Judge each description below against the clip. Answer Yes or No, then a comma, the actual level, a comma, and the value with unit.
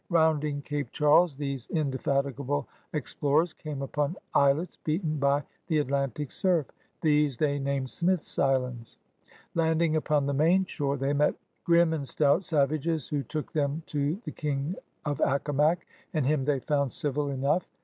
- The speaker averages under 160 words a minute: Yes, average, 150 wpm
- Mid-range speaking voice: Yes, medium, 145 Hz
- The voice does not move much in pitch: Yes, narrow, 2.2 semitones